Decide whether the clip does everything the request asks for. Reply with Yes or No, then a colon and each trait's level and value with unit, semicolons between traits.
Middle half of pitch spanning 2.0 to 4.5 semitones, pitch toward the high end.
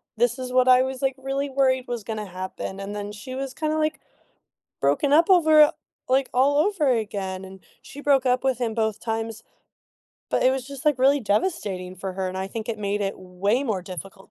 No: average, 5.2 semitones; high, 245 Hz